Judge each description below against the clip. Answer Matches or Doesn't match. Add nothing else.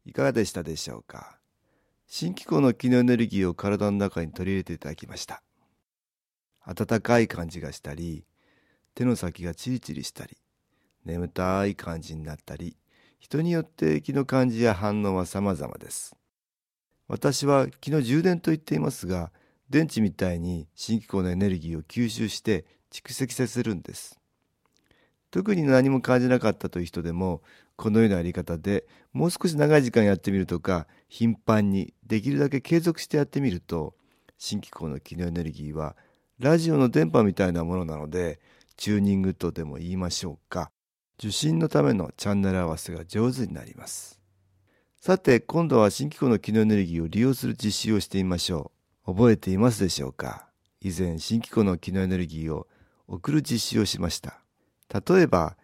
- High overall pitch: Doesn't match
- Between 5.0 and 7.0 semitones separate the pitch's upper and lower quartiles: Matches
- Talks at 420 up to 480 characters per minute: Doesn't match